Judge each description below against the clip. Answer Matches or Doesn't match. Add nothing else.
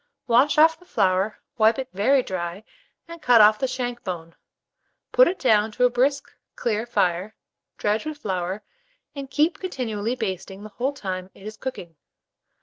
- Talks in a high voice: Matches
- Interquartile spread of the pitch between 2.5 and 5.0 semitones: Doesn't match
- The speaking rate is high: Doesn't match